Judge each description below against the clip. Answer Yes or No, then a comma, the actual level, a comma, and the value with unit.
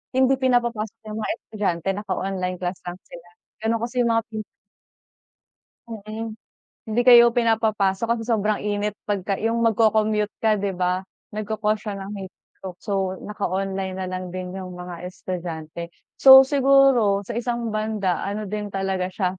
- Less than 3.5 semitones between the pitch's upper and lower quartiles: Yes, average, 3.1 semitones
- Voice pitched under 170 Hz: No, high, 210 Hz